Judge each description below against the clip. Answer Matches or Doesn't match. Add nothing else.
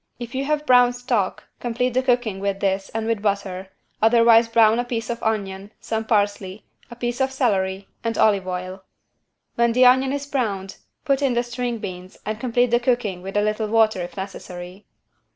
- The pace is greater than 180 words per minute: Matches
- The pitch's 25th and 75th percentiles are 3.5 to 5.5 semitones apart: Matches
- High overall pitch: Matches